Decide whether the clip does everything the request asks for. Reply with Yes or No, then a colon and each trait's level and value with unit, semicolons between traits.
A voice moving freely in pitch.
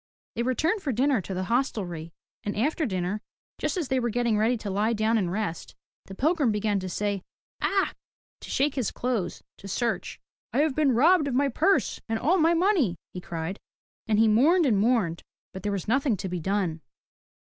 Yes: wide, 5.9 semitones